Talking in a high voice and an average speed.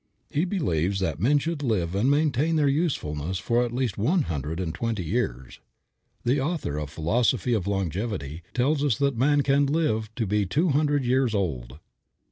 No: low, 115 Hz; average, 175 wpm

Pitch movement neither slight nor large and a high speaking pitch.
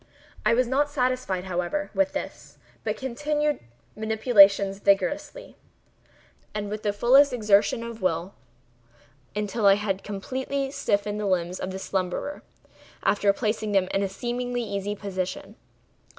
Yes: average, 4.5 semitones; high, 210 Hz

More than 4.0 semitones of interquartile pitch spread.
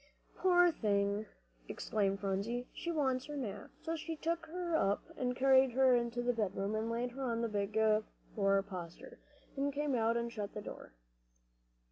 Yes: average, 5.1 semitones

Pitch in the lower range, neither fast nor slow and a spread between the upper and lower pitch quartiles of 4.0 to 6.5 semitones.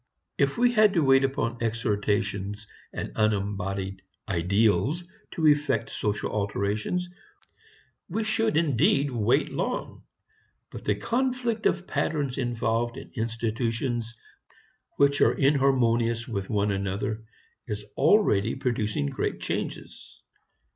No: low, 115 Hz; slow, 110 wpm; wide, 5.5 semitones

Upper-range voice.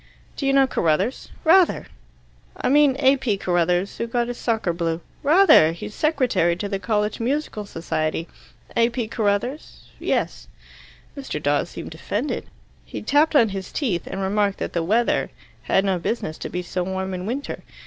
Yes: high, 210 Hz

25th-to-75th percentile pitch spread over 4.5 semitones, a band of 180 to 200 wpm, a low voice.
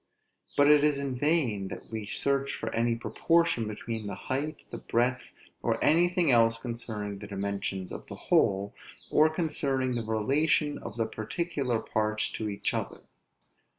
No: average, 5.3 semitones; average, 160 wpm; low, 120 Hz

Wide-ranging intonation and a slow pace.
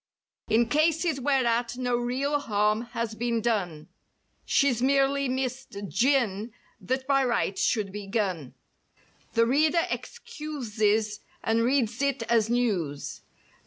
No: average, 3.9 semitones; slow, 120 wpm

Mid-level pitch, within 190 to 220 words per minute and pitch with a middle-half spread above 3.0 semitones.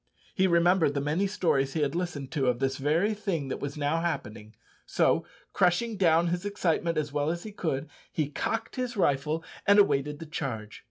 Yes: medium, 160 Hz; average, 195 wpm; average, 4.4 semitones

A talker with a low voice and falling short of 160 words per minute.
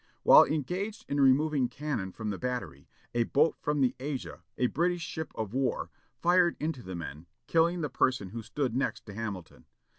No: low, 130 Hz; average, 180 wpm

